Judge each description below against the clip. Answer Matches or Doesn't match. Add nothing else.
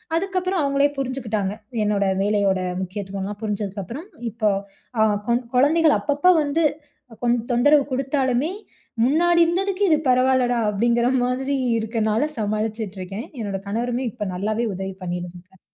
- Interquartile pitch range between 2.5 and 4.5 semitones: Doesn't match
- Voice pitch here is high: Matches